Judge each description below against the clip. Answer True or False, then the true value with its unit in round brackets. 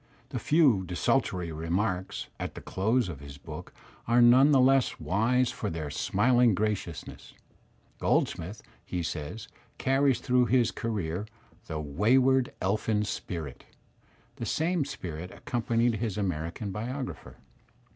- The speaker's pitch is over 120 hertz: False (110 Hz)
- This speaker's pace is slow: True (125 wpm)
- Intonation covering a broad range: True (6.0 semitones)